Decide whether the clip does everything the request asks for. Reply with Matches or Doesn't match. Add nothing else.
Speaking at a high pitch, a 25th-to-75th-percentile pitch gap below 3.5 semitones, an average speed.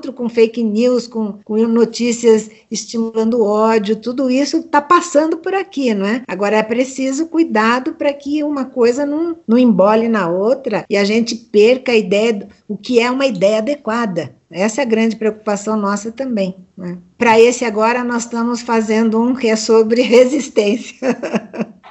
Matches